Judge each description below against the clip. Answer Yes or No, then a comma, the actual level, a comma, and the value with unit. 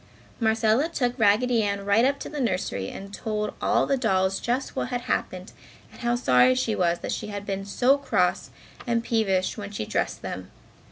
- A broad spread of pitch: No, average, 3.8 semitones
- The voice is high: Yes, high, 215 Hz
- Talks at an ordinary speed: Yes, average, 190 wpm